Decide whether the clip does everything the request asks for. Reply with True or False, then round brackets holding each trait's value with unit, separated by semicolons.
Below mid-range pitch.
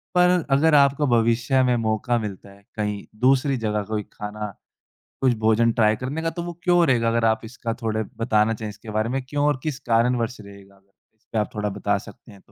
True (115 Hz)